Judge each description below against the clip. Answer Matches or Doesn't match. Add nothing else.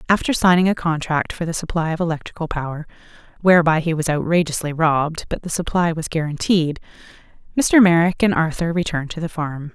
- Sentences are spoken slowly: Doesn't match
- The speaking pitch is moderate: Matches